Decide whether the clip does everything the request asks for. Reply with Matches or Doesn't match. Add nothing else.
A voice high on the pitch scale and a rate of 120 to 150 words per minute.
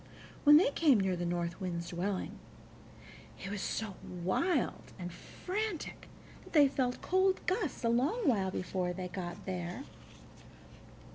Matches